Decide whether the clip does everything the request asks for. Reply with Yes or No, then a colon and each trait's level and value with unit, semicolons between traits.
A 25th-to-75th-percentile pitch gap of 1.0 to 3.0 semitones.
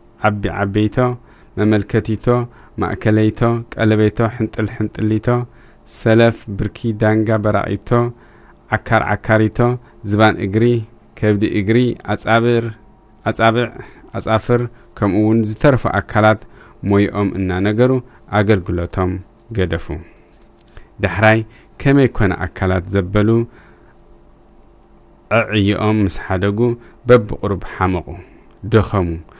Yes: narrow, 2.4 semitones